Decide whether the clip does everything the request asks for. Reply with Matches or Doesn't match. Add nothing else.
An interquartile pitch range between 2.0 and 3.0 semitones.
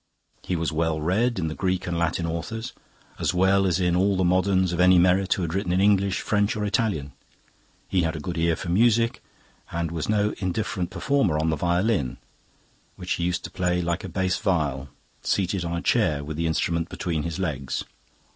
Matches